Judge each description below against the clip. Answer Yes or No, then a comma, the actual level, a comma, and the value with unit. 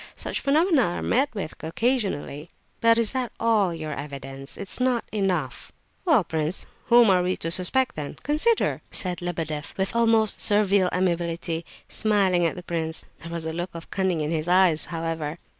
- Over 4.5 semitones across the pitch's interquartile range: Yes, wide, 5.4 semitones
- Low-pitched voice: No, medium, 180 Hz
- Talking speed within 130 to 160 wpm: No, average, 175 wpm